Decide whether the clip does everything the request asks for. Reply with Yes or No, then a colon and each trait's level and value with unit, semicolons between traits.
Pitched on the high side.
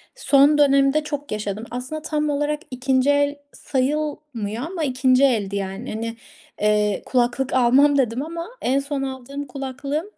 Yes: very high, 270 Hz